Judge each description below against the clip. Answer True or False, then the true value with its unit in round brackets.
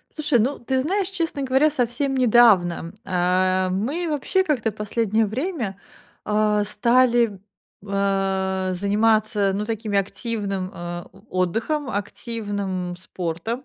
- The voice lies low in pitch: False (215 Hz)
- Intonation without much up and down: False (4.8 semitones)